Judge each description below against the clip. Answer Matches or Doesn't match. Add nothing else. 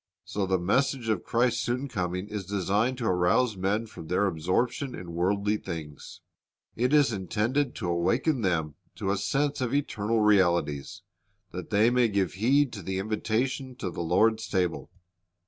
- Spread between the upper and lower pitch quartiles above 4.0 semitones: Matches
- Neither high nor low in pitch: Doesn't match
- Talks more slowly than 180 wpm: Matches